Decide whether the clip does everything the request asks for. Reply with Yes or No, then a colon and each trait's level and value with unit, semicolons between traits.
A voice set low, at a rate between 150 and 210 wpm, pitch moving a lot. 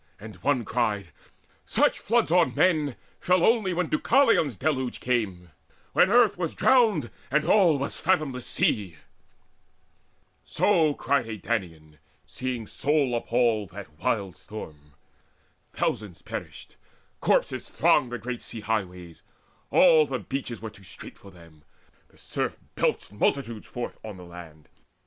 No: low, 120 Hz; slow, 135 wpm; wide, 7.6 semitones